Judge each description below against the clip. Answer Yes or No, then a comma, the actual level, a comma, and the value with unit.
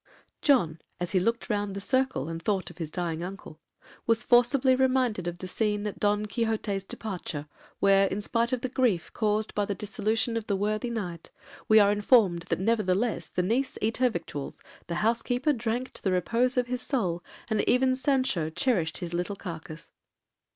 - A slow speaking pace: No, average, 185 wpm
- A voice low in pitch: No, high, 210 Hz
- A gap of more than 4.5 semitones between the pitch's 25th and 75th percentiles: Yes, average, 5.0 semitones